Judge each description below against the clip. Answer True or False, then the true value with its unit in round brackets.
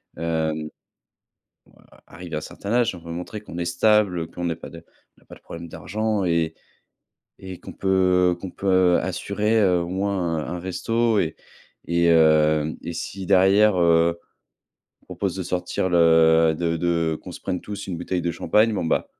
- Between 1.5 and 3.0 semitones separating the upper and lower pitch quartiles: True (2.6 semitones)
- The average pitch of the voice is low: True (90 Hz)